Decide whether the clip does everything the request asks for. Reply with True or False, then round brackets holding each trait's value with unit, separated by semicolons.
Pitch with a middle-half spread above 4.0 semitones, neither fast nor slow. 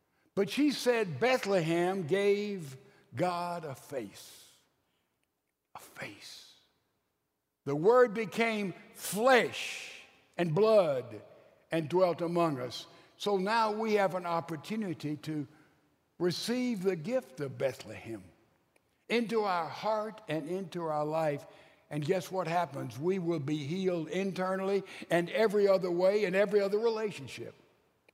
False (4.7 semitones; 120 wpm)